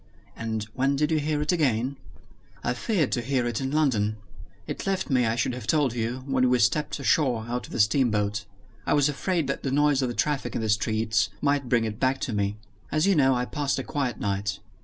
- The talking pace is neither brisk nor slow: No, fast, 225 wpm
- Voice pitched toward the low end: Yes, low, 130 Hz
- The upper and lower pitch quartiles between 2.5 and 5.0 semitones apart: Yes, average, 4.3 semitones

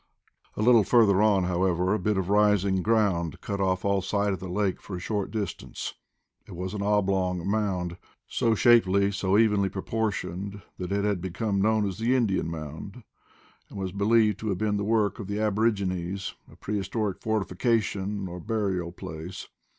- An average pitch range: No, narrow, 2.3 semitones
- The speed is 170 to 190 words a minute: Yes, average, 175 wpm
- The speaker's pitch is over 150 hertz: No, low, 100 Hz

